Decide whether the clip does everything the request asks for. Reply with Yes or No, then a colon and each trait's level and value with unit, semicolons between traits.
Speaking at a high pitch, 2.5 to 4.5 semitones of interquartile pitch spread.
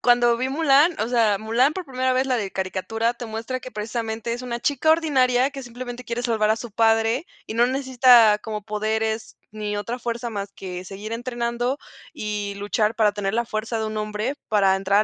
Yes: high, 230 Hz; average, 2.9 semitones